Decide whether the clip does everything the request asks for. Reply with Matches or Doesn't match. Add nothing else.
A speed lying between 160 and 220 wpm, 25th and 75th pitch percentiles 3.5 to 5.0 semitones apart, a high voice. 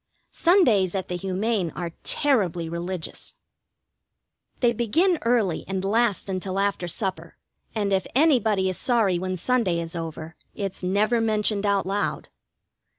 Doesn't match